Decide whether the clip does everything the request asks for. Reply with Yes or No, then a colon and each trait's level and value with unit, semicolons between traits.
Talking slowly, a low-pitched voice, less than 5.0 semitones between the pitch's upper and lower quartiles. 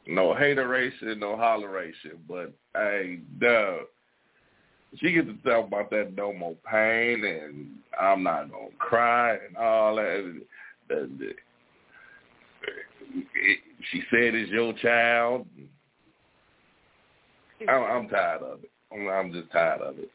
Yes: slow, 115 wpm; low, 115 Hz; average, 2.7 semitones